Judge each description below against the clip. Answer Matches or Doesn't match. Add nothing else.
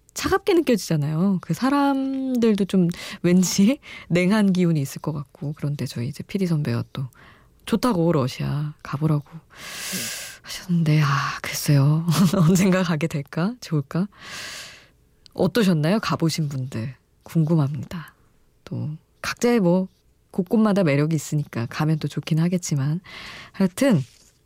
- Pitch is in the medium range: Matches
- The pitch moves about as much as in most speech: Matches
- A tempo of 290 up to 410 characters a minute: Doesn't match